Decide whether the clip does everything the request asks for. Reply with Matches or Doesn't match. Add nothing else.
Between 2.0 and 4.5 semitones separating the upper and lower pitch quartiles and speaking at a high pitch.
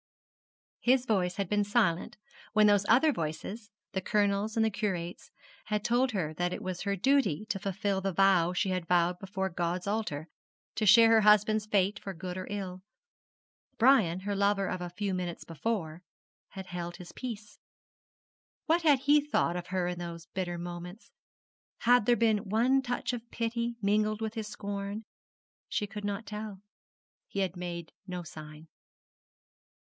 Matches